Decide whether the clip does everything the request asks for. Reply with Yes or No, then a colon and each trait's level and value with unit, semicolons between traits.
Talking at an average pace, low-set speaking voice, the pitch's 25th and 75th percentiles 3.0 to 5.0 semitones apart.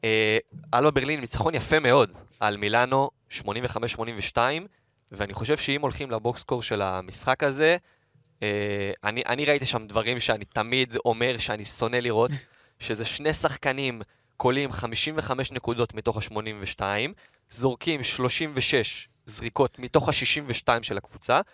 Yes: average, 125 wpm; low, 120 Hz; average, 3.9 semitones